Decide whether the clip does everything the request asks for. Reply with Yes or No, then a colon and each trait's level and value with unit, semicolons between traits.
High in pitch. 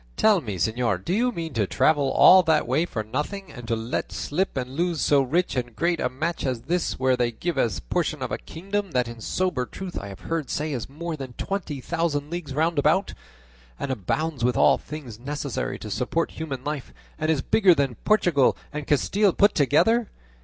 No: medium, 150 Hz